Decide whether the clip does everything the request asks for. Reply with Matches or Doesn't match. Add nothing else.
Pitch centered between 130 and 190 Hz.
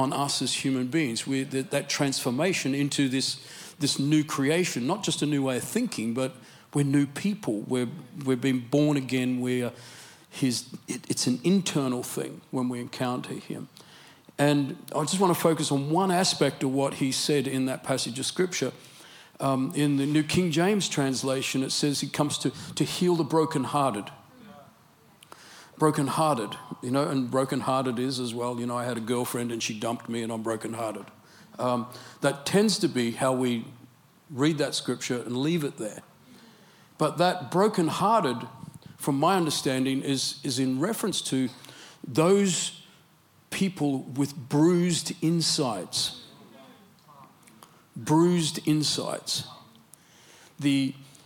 Matches